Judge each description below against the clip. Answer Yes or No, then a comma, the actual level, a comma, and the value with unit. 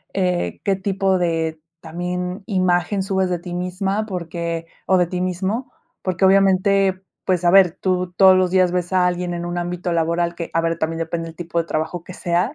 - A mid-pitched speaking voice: Yes, medium, 180 Hz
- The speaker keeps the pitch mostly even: Yes, narrow, 1.7 semitones